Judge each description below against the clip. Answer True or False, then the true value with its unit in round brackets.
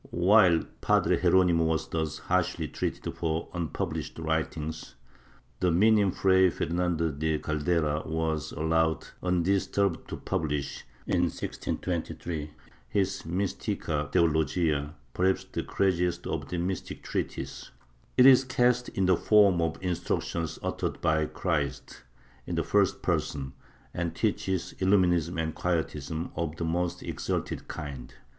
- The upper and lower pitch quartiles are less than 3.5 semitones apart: True (2.6 semitones)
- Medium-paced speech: False (125 wpm)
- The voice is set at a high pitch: False (85 Hz)